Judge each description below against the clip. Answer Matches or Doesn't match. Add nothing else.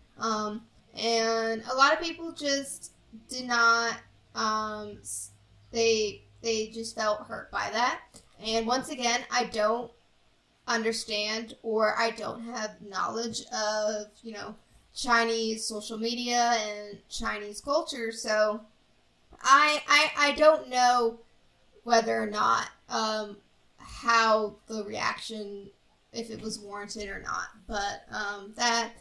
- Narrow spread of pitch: Matches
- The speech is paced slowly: Matches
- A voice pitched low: Doesn't match